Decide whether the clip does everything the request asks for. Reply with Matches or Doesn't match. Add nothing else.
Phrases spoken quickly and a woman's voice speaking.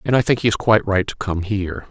Doesn't match